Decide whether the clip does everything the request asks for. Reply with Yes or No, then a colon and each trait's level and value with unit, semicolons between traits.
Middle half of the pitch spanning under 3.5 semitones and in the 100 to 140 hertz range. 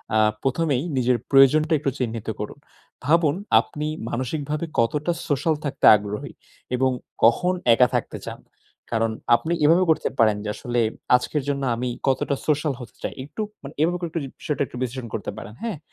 No: average, 4.1 semitones; low, 135 Hz